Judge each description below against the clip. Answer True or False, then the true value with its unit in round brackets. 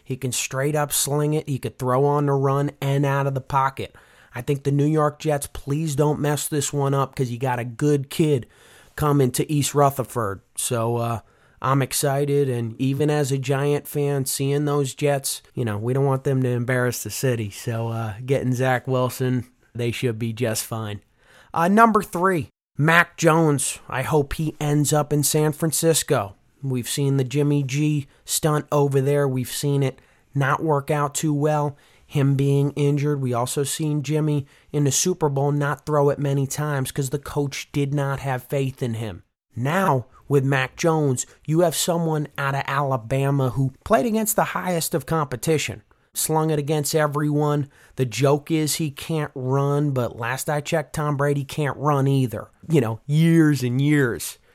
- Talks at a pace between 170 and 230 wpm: True (185 wpm)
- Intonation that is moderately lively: False (2.3 semitones)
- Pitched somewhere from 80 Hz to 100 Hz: False (140 Hz)